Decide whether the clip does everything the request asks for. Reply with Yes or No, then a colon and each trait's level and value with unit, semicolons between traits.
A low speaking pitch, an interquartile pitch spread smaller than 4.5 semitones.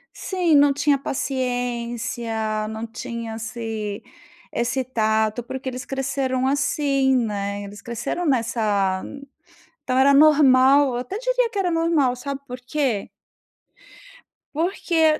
No: very high, 255 Hz; average, 4.0 semitones